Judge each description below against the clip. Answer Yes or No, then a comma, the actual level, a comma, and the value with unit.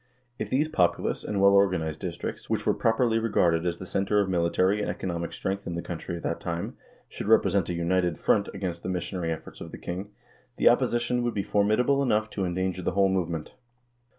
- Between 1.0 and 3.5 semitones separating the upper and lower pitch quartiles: Yes, average, 3.2 semitones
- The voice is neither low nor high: No, very low, 95 Hz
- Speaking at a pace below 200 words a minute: No, fast, 205 wpm